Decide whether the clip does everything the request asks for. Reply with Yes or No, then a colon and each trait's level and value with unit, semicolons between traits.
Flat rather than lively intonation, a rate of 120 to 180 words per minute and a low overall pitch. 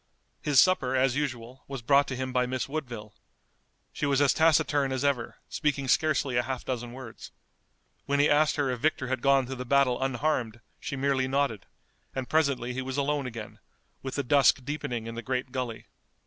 No: narrow, 2.2 semitones; average, 190 wpm; low, 130 Hz